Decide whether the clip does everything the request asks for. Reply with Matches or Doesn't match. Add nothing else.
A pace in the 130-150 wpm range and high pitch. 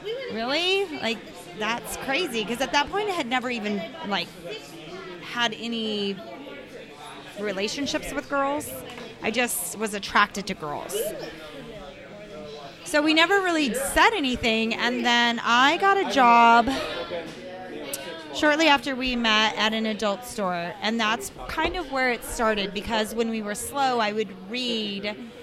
Matches